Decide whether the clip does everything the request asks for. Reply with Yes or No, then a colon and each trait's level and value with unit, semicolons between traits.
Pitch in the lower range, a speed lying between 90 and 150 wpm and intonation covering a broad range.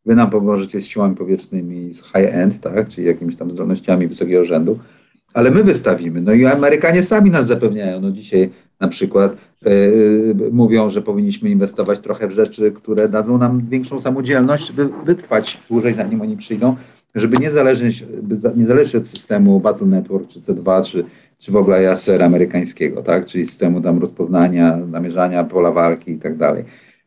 No: low, 110 Hz; fast, 160 wpm; wide, 7.4 semitones